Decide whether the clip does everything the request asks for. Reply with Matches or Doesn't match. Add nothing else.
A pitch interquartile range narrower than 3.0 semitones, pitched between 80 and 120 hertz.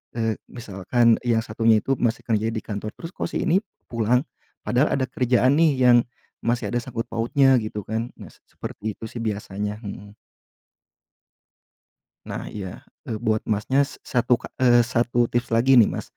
Matches